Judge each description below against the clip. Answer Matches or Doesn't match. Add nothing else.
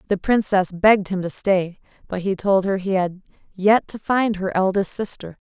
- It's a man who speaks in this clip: Doesn't match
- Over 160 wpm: Matches